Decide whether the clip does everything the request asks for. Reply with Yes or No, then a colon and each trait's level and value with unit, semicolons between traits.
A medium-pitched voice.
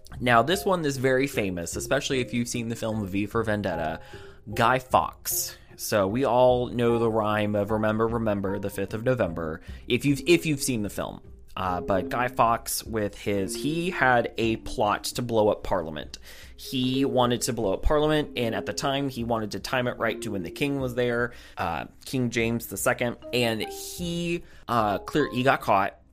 No: low, 120 Hz